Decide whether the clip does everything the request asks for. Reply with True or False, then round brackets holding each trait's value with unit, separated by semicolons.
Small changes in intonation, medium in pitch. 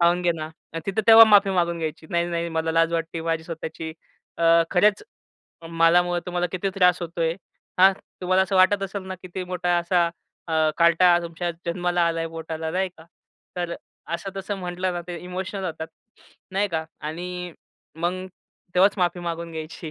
True (1.9 semitones; 175 Hz)